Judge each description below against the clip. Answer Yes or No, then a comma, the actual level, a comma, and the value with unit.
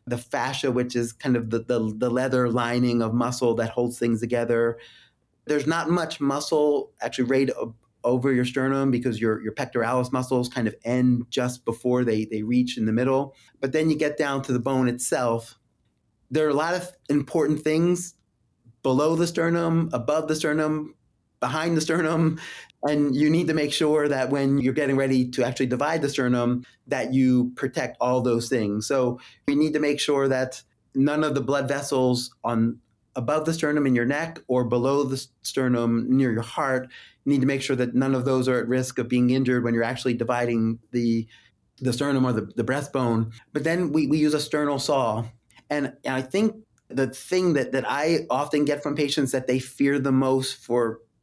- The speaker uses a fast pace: No, average, 195 wpm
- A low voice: Yes, low, 130 Hz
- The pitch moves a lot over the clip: No, average, 3.2 semitones